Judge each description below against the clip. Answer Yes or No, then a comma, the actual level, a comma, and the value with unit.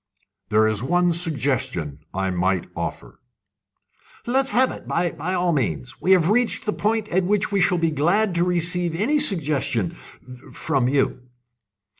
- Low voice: No, medium, 170 Hz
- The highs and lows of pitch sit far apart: Yes, wide, 7.0 semitones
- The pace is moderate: Yes, average, 150 wpm